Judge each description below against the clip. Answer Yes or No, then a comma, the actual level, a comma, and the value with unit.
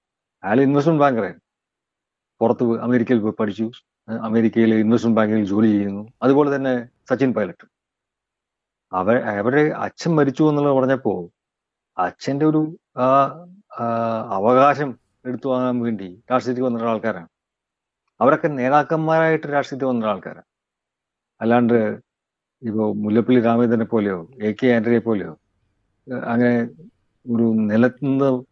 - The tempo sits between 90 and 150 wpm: Yes, average, 95 wpm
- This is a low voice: Yes, low, 120 Hz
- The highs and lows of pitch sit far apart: No, average, 3.4 semitones